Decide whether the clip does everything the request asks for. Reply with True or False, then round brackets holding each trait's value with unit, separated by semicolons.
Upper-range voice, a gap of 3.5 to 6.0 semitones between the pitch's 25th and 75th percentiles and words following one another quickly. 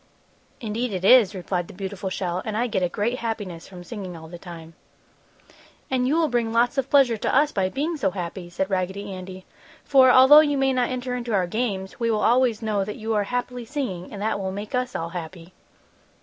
True (210 Hz; 5.0 semitones; 220 wpm)